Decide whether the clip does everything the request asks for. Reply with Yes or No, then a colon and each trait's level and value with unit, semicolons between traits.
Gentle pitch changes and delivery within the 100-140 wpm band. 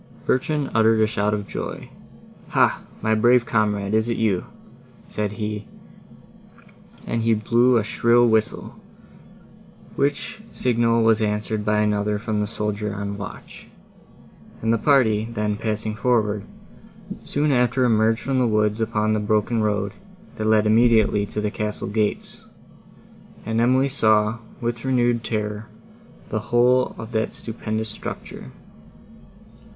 Yes: narrow, 1.9 semitones; slow, 135 wpm